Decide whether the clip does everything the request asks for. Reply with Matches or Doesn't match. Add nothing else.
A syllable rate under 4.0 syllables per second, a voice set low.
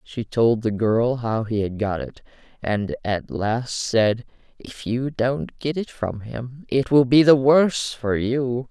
Matches